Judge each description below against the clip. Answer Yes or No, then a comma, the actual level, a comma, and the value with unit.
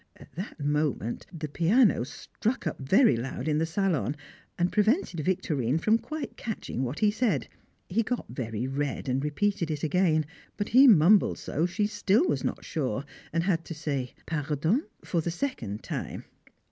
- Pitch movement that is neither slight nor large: No, wide, 6.3 semitones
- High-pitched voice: No, medium, 165 Hz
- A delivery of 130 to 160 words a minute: No, average, 170 wpm